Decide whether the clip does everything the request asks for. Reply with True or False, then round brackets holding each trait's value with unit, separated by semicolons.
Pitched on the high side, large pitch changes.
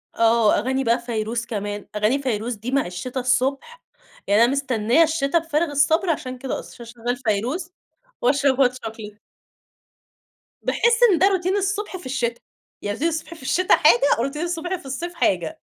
True (260 Hz; 5.8 semitones)